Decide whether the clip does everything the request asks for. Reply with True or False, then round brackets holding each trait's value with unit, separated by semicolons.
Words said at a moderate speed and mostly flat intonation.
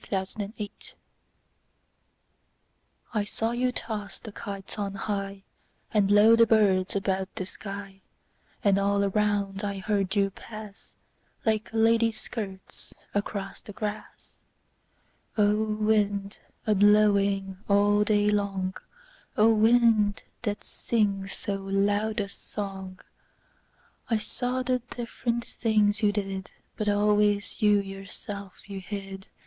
False (105 wpm; 1.6 semitones)